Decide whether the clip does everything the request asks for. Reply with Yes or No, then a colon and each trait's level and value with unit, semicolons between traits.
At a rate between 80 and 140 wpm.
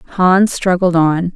Yes: slow, 135 wpm